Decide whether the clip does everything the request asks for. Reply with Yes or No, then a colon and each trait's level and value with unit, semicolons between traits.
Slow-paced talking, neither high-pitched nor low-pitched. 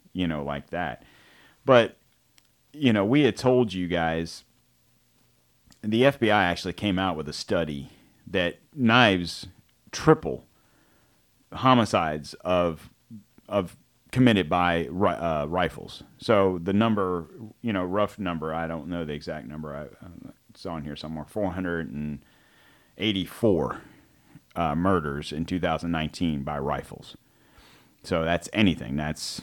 No: slow, 130 wpm; very low, 90 Hz